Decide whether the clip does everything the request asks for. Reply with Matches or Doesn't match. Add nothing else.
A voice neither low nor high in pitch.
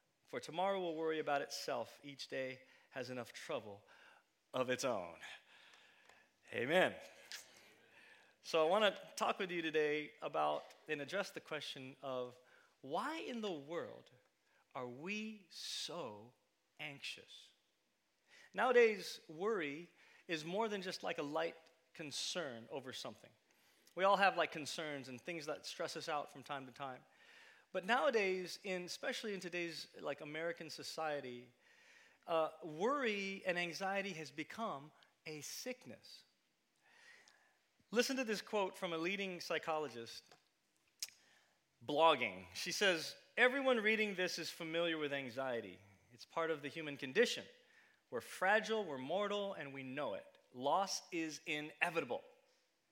Matches